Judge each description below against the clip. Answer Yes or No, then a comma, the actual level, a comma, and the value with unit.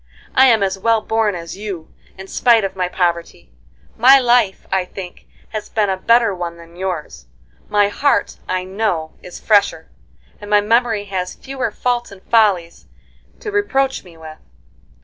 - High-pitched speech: Yes, high, 200 Hz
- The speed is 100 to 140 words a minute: No, average, 165 wpm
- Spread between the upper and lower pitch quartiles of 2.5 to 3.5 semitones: No, average, 4.1 semitones